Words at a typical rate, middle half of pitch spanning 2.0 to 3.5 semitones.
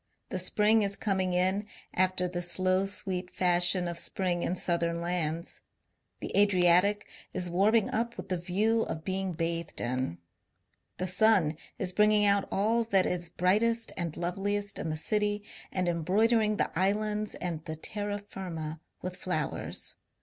Yes: average, 150 wpm; average, 2.9 semitones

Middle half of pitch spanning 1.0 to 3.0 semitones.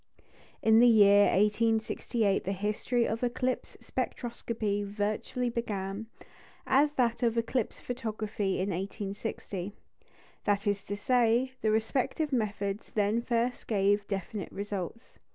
Yes: average, 2.7 semitones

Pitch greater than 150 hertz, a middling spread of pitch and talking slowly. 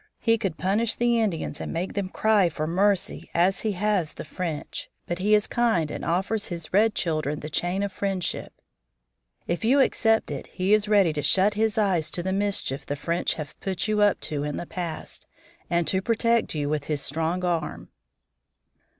No: medium, 185 Hz; average, 4.4 semitones; average, 195 wpm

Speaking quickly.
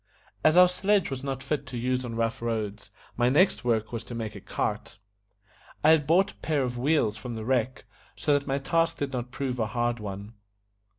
Yes: fast, 215 wpm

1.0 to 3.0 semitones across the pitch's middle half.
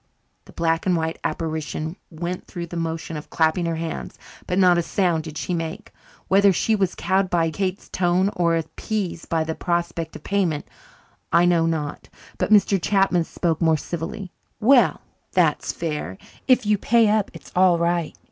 Yes: narrow, 2.6 semitones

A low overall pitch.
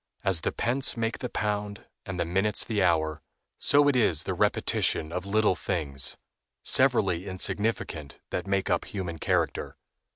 Yes: very low, 95 Hz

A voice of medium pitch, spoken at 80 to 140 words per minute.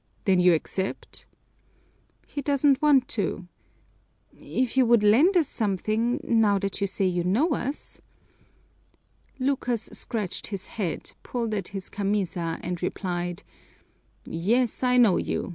No: high, 210 Hz; slow, 135 wpm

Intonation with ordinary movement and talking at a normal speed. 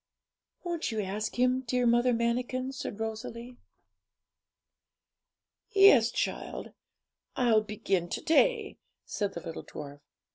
No: average, 3.2 semitones; slow, 110 wpm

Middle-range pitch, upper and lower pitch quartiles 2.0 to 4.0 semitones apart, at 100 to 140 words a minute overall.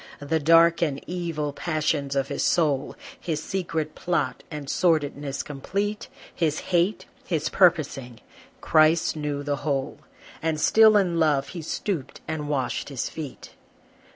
Yes: medium, 155 Hz; average, 3.0 semitones; slow, 135 wpm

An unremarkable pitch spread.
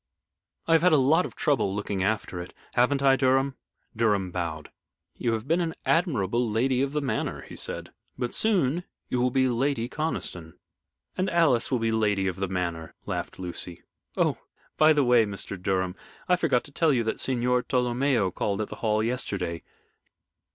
No: wide, 5.9 semitones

